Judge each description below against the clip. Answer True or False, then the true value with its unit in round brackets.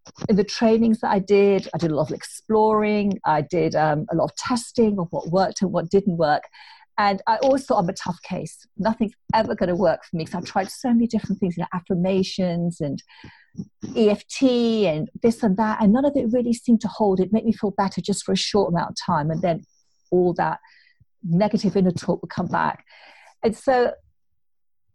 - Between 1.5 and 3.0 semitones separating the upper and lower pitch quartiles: False (3.7 semitones)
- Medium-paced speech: False (215 wpm)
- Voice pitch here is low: False (200 Hz)